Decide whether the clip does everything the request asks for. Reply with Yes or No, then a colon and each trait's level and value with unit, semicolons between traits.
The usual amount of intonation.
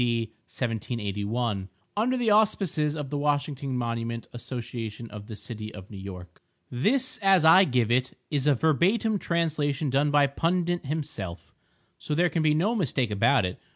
No: wide, 6.2 semitones